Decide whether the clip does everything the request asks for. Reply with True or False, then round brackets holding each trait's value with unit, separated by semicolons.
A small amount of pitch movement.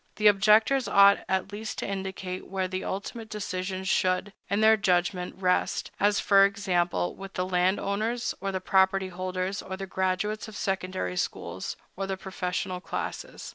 True (1.6 semitones)